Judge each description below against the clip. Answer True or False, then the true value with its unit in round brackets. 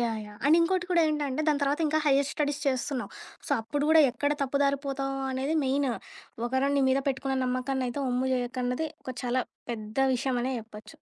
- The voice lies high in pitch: True (270 Hz)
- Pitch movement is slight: True (2.3 semitones)